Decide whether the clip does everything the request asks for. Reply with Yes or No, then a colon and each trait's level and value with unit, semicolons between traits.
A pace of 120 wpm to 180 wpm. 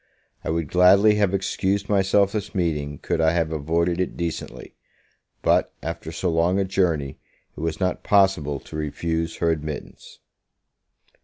Yes: average, 150 wpm